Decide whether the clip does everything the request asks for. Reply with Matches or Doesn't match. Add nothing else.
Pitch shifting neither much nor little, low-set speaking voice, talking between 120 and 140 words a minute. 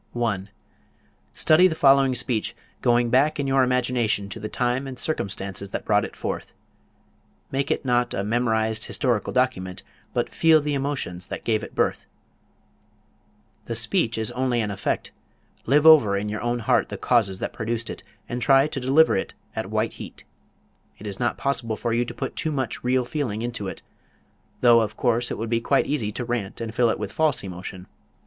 Doesn't match